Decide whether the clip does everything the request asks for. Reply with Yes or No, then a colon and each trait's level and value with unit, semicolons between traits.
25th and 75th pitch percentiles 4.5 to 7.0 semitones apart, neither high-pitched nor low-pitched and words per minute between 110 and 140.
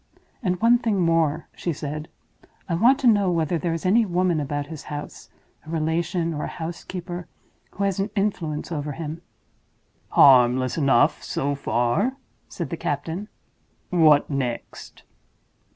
No: average, 3.7 semitones; medium, 165 Hz; slow, 135 wpm